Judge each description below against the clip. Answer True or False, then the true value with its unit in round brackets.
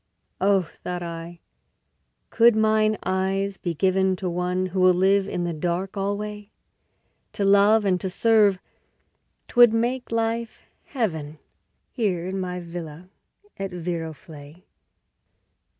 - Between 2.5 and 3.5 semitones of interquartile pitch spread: True (3.0 semitones)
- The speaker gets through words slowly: True (120 wpm)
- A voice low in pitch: False (190 Hz)